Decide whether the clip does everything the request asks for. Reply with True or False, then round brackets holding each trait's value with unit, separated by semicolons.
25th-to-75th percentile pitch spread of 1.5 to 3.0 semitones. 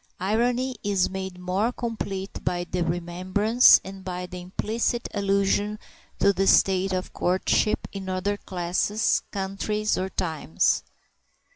True (2.4 semitones)